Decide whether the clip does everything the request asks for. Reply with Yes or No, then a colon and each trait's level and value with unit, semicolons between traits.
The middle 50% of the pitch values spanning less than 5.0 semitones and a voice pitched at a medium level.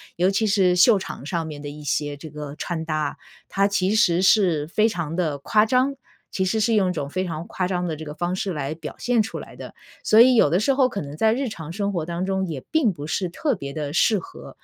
No: average, 5.3 semitones; medium, 180 Hz